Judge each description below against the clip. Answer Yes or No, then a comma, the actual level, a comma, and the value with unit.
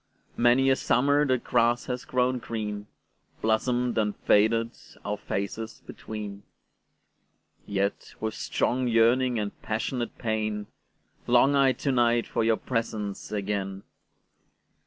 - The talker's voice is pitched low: Yes, low, 115 Hz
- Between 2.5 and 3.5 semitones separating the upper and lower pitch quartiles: Yes, average, 2.9 semitones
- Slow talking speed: Yes, slow, 105 wpm